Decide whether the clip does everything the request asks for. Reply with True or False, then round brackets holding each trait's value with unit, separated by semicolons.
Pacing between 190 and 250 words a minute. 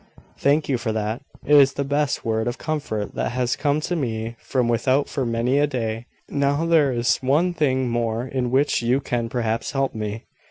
True (200 wpm)